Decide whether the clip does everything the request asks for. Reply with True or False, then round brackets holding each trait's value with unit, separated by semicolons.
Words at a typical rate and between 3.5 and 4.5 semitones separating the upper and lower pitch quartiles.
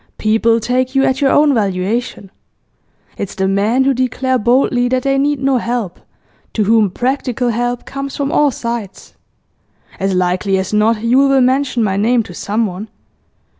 True (165 wpm; 3.9 semitones)